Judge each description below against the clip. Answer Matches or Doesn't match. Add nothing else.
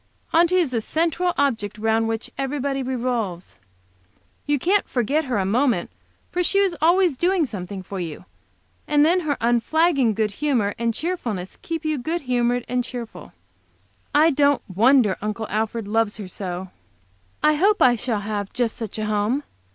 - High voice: Matches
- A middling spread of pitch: Doesn't match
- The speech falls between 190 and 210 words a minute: Doesn't match